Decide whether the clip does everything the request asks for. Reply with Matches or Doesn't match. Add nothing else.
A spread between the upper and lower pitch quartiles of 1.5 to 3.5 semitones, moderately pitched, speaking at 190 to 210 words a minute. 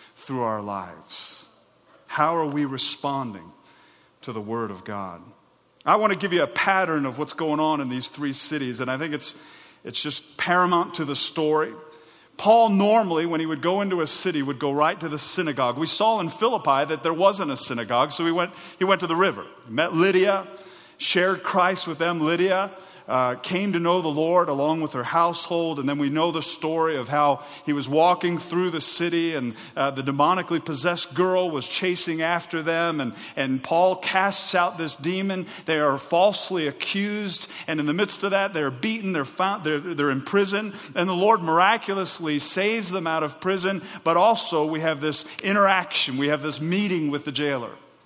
Doesn't match